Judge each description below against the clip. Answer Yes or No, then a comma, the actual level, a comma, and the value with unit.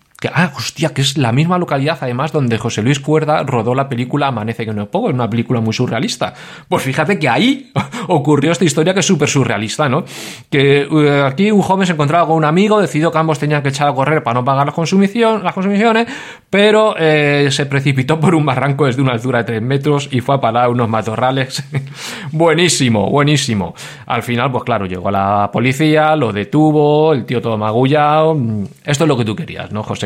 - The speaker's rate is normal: No, fast, 210 wpm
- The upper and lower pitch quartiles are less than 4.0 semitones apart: No, average, 4.5 semitones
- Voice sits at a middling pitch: Yes, medium, 145 Hz